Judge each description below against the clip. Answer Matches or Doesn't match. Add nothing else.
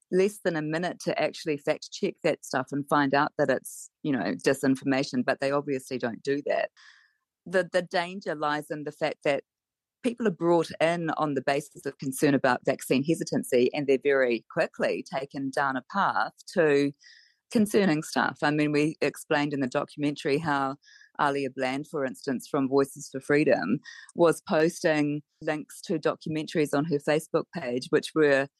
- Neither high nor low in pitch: Matches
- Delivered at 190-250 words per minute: Doesn't match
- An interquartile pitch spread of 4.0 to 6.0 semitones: Doesn't match